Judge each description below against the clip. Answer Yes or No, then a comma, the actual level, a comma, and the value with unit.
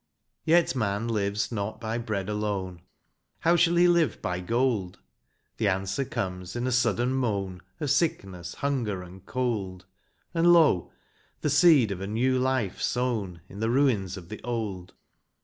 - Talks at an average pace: Yes, average, 160 wpm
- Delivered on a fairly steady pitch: No, average, 5.2 semitones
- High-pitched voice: No, low, 110 Hz